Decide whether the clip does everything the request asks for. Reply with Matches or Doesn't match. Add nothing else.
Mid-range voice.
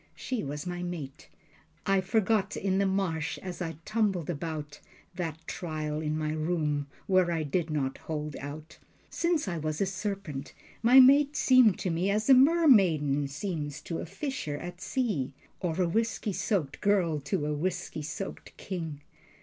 Matches